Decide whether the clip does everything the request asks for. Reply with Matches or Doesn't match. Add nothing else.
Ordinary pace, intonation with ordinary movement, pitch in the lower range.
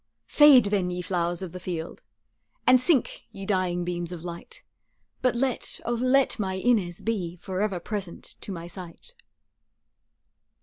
Doesn't match